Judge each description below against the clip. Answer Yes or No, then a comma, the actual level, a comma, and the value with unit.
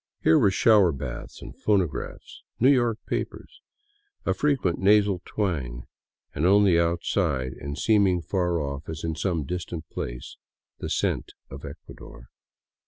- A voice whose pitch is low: Yes, very low, 85 Hz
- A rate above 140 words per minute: No, slow, 135 wpm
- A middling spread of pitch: No, wide, 5.8 semitones